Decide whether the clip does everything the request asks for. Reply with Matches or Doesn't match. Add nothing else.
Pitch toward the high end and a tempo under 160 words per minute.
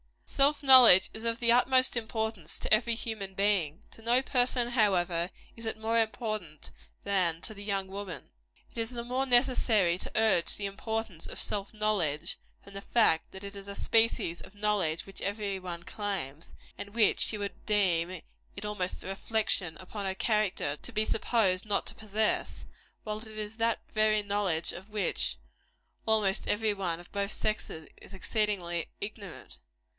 Doesn't match